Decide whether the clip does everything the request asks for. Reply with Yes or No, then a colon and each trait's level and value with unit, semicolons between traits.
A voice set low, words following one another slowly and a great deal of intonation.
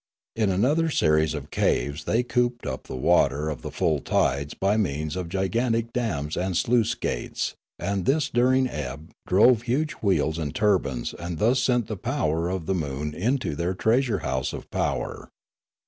No: very low, 95 Hz; average, 175 wpm; wide, 7.8 semitones